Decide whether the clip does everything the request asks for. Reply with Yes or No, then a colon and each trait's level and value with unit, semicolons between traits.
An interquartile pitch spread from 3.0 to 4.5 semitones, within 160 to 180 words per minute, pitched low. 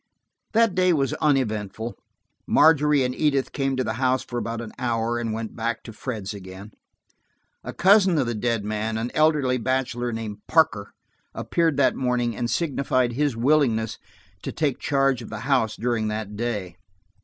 Yes: average, 3.8 semitones; average, 165 wpm; low, 120 Hz